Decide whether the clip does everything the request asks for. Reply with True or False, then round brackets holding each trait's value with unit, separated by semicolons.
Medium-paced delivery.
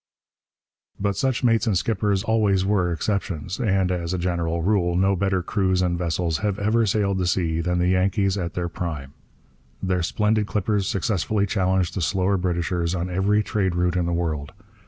True (180 wpm)